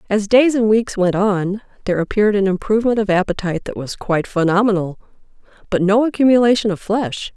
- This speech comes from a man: No, female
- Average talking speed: Yes, average, 170 wpm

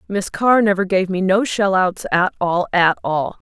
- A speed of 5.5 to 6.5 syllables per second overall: No, 4.3 syllables/s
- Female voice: Yes, female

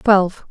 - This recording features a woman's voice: Yes, female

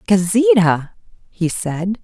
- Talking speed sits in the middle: No, slow, 90 wpm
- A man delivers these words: No, female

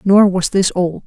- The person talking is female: Yes, female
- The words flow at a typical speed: No, fast, 225 wpm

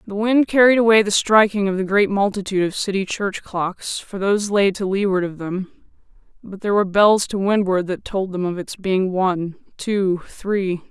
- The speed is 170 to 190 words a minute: Yes, average, 185 wpm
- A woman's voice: Yes, female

